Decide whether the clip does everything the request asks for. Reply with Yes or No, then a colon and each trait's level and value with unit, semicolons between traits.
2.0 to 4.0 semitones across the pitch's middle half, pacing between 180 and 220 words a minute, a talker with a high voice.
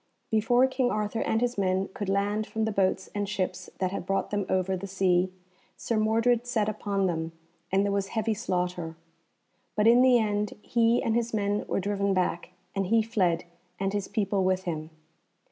Yes: average, 2.8 semitones; average, 190 wpm; high, 205 Hz